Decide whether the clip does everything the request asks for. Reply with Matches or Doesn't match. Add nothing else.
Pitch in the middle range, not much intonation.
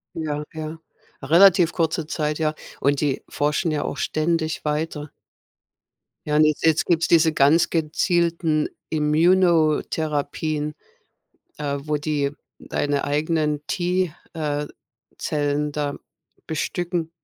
Matches